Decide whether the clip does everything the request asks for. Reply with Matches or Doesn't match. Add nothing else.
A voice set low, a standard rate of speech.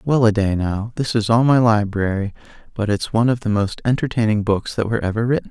Doesn't match